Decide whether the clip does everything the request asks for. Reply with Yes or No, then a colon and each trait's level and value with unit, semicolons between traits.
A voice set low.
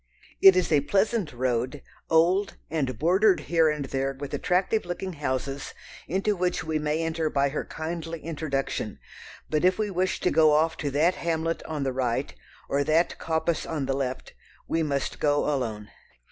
No: medium, 155 Hz